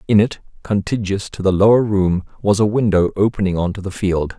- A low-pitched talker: Yes, low, 100 Hz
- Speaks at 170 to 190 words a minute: No, fast, 205 wpm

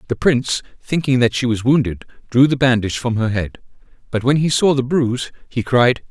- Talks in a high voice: No, low, 125 Hz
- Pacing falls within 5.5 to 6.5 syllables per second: Yes, 5.6 syllables/s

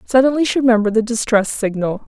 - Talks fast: No, average, 165 wpm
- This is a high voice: Yes, high, 230 Hz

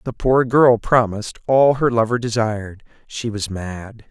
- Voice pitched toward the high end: No, low, 115 Hz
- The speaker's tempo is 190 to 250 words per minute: No, average, 160 wpm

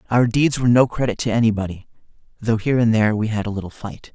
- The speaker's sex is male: Yes, male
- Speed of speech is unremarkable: No, fast, 230 wpm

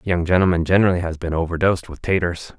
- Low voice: Yes, very low, 85 Hz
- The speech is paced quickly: No, average, 185 wpm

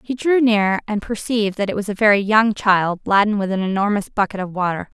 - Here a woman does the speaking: Yes, female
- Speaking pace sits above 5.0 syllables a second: Yes, 5.8 syllables/s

